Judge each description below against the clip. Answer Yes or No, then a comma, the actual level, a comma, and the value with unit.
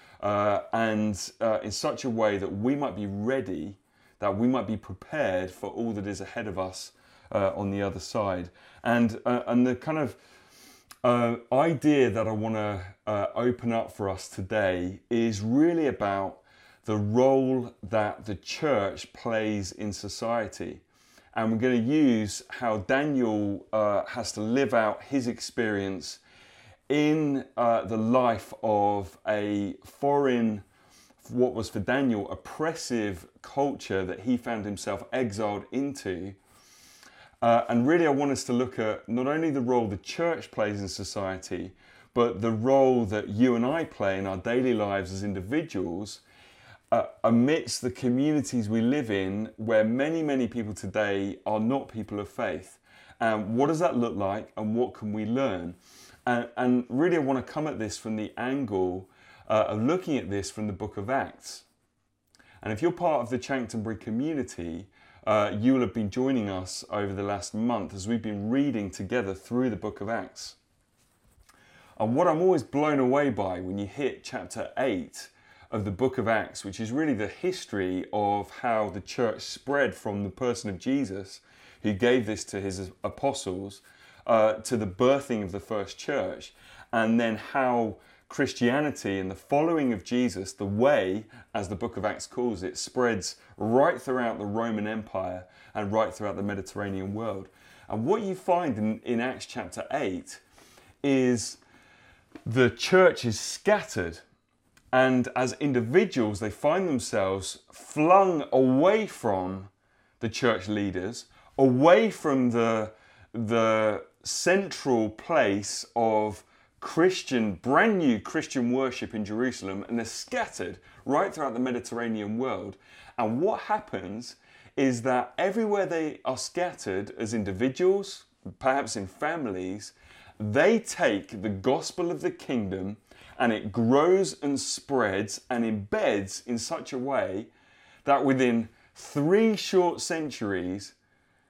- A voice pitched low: Yes, low, 115 Hz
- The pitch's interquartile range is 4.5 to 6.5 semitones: No, average, 4.1 semitones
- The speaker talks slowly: No, average, 155 wpm